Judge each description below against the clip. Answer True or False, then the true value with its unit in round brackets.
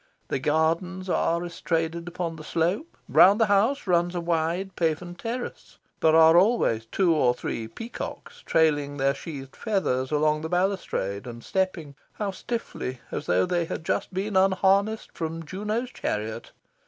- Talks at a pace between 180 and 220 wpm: False (155 wpm)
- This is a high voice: False (170 Hz)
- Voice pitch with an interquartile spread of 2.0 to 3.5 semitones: False (4.0 semitones)